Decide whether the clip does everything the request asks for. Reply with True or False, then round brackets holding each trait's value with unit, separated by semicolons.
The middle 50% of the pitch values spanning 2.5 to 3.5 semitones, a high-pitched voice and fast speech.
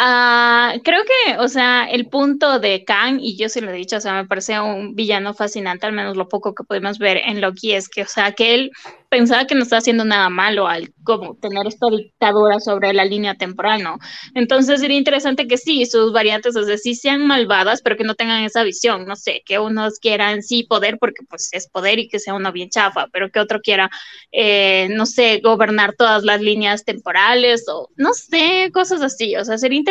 True (3.0 semitones; 220 Hz; 220 wpm)